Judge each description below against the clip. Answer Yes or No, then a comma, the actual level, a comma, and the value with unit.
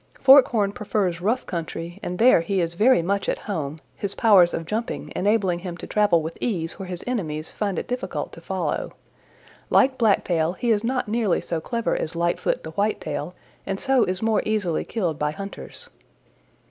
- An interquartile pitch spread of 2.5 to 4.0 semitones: No, average, 4.4 semitones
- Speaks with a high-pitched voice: Yes, high, 195 Hz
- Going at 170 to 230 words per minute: Yes, average, 185 wpm